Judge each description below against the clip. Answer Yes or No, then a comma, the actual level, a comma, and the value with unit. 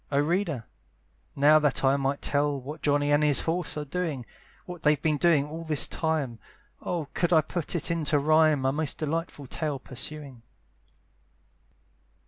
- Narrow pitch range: Yes, narrow, 2.3 semitones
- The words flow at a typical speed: Yes, average, 160 wpm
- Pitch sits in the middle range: Yes, medium, 150 Hz